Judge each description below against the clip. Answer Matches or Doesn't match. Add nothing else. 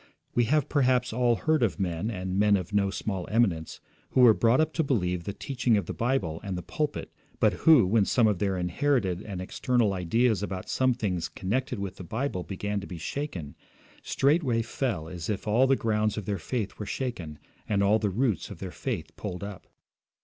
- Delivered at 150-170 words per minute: Doesn't match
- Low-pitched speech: Matches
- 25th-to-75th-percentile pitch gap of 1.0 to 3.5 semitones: Doesn't match